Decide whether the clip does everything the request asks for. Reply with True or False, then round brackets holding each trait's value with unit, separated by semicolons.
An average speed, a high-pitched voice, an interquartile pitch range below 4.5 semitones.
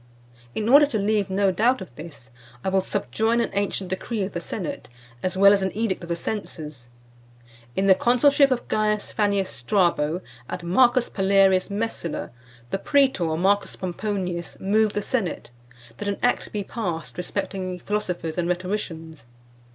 True (160 wpm; 195 Hz; 3.2 semitones)